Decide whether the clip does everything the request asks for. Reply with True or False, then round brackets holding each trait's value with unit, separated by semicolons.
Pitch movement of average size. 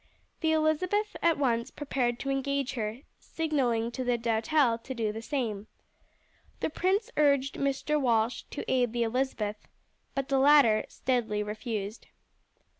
True (4.0 semitones)